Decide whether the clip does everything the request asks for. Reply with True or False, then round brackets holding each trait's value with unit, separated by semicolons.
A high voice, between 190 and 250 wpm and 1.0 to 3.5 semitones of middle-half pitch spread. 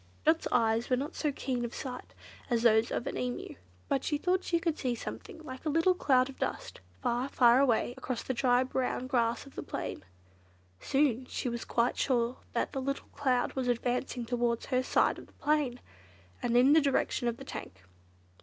True (255 Hz; 200 wpm; 2.5 semitones)